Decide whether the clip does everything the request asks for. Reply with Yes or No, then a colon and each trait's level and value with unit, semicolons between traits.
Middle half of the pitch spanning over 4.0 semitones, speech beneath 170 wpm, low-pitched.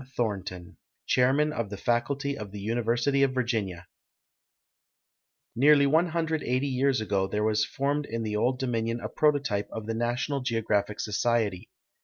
Yes: average, 4.5 semitones; average, 140 wpm; low, 120 Hz